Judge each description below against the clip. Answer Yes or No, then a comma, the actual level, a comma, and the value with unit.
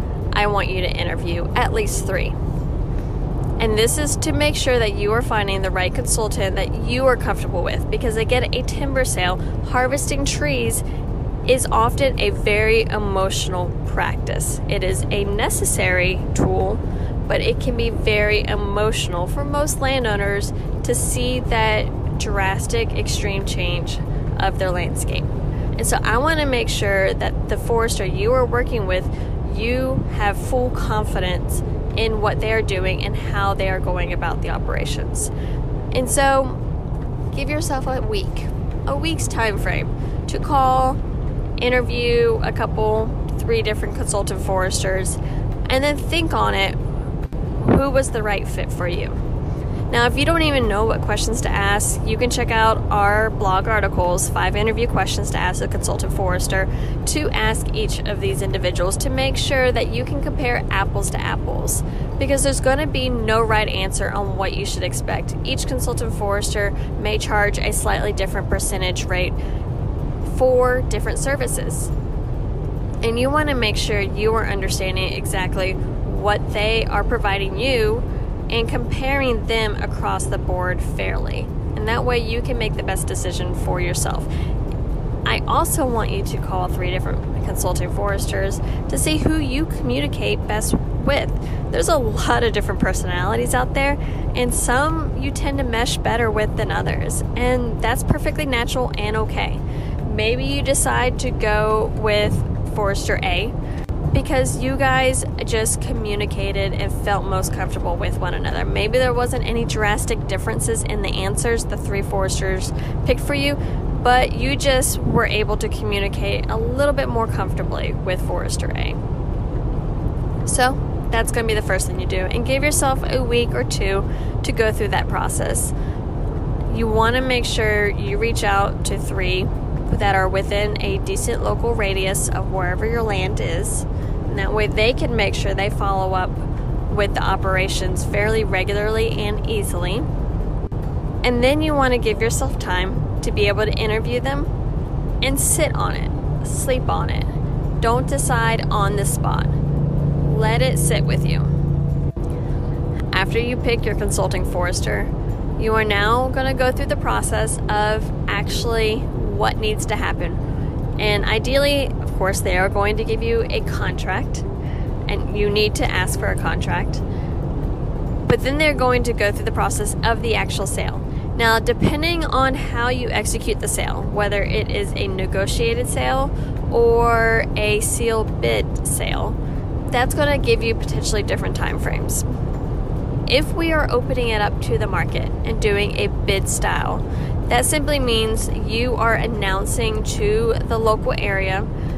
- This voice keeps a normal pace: Yes, average, 160 wpm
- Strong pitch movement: No, average, 3.9 semitones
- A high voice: No, low, 110 Hz